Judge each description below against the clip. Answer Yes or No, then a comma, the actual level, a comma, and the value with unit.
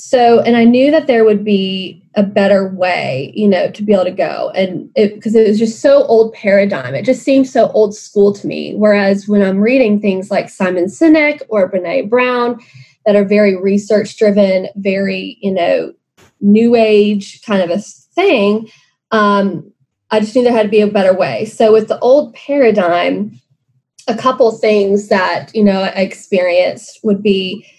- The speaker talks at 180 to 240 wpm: Yes, average, 185 wpm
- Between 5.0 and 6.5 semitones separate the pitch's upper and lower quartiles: No, average, 2.8 semitones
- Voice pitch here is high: Yes, high, 205 Hz